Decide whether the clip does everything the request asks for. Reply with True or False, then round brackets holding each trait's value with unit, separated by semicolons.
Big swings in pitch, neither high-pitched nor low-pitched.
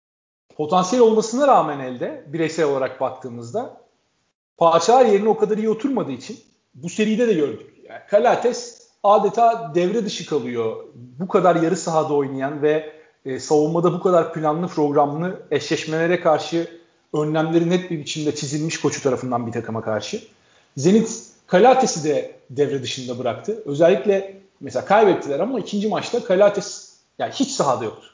True (6.3 semitones; 170 Hz)